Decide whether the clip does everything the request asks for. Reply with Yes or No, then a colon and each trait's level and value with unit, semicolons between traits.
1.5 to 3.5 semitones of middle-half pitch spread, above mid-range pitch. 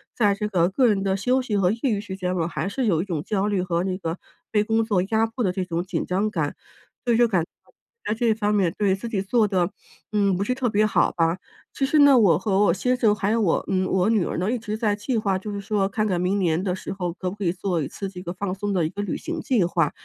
Yes: average, 2.9 semitones; high, 200 Hz